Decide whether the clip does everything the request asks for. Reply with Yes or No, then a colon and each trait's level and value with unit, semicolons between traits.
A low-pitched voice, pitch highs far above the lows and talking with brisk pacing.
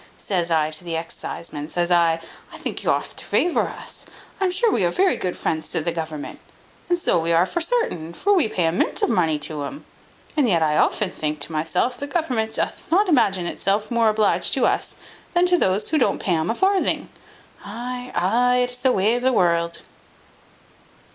No: high, 195 Hz; wide, 7.3 semitones; fast, 215 wpm